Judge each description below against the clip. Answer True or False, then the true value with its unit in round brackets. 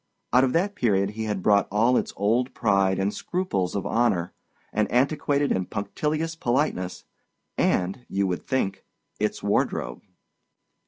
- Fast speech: False (145 wpm)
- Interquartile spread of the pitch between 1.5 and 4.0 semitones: False (5.3 semitones)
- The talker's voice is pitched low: True (110 Hz)